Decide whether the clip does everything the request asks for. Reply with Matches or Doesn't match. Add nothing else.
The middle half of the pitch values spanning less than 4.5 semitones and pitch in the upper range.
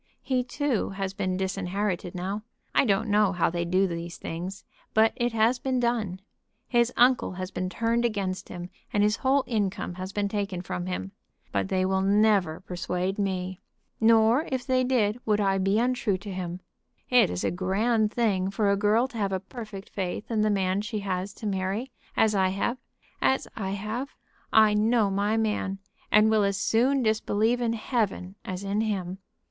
Matches